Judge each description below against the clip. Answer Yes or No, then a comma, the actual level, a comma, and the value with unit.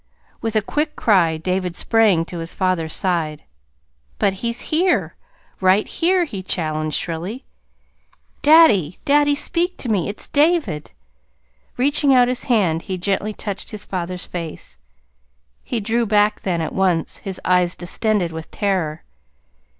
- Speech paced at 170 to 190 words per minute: No, average, 140 wpm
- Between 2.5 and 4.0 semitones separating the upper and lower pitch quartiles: No, wide, 5.6 semitones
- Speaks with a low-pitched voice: No, high, 195 Hz